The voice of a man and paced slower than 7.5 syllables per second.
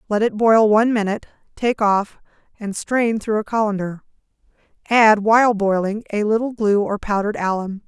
No: female; 5.3 syllables/s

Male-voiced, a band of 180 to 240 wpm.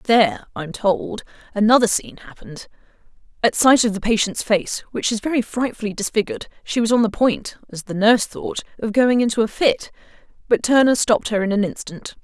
No: female; average, 185 wpm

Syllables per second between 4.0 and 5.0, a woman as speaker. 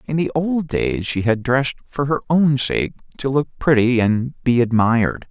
No: 4.5 syllables/s; male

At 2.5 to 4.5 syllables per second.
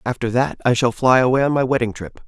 No: 6.1 syllables/s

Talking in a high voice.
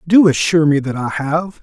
No: medium, 150 Hz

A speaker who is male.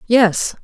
No: female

